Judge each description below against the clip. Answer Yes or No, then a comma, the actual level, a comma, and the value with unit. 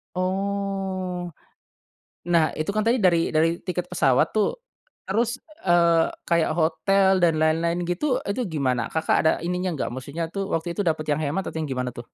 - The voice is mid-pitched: Yes, medium, 170 Hz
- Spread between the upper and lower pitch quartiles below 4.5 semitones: Yes, average, 3.3 semitones